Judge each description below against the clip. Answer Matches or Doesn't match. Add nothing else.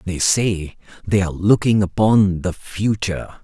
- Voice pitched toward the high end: Doesn't match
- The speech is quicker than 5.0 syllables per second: Doesn't match